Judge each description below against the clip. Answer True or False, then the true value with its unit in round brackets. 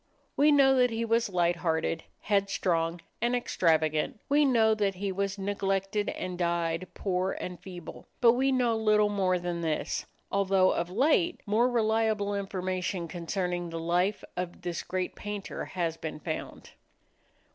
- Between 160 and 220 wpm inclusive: False (150 wpm)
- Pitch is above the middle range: True (195 Hz)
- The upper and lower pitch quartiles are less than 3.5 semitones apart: False (3.8 semitones)